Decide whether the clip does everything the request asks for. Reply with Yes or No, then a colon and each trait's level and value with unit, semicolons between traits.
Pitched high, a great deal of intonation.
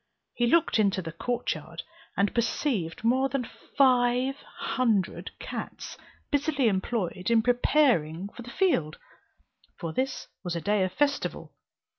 Yes: high, 240 Hz; wide, 6.0 semitones